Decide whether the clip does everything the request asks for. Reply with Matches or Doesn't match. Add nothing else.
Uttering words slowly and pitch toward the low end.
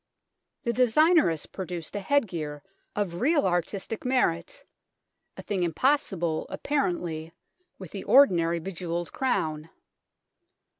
Doesn't match